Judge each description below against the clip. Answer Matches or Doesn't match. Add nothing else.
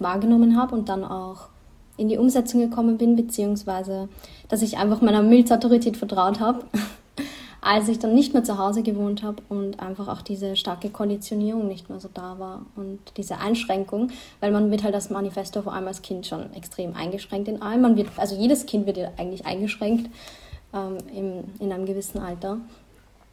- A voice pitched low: Doesn't match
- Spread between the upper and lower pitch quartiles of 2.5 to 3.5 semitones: Matches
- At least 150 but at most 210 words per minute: Matches